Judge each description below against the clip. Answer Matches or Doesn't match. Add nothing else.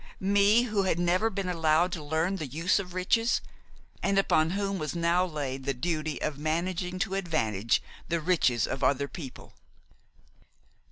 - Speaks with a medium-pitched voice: Matches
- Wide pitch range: Doesn't match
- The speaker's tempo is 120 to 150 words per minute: Doesn't match